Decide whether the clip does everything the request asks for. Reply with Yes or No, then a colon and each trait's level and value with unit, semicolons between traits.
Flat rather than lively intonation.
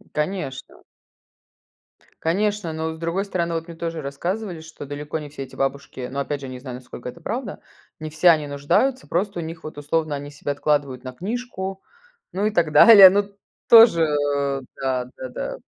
No: average, 4.7 semitones